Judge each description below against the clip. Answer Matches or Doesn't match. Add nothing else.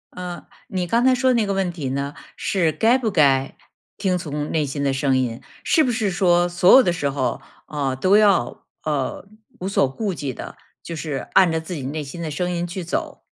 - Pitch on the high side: Doesn't match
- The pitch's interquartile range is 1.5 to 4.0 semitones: Doesn't match